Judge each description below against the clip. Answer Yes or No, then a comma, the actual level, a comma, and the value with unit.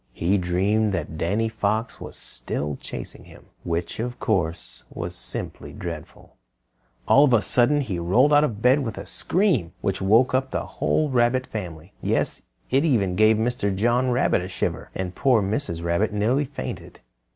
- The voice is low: Yes, low, 110 Hz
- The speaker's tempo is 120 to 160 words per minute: No, average, 170 wpm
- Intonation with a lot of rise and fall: Yes, wide, 5.9 semitones